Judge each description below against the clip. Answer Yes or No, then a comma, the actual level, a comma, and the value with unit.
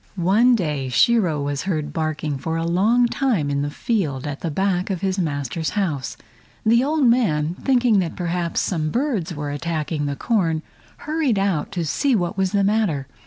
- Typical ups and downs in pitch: No, wide, 6.1 semitones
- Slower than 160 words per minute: No, average, 180 wpm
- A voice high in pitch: No, medium, 175 Hz